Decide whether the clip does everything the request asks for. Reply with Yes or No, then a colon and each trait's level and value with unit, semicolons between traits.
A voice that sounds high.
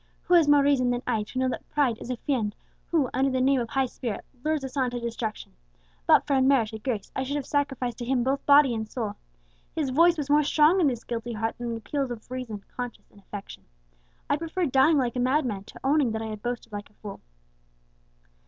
Yes: very high, 255 Hz